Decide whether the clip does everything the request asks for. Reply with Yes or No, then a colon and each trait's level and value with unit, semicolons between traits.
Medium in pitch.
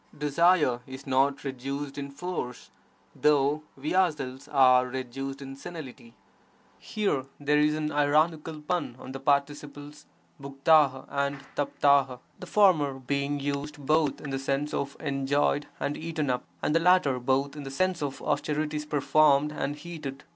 Yes: medium, 145 Hz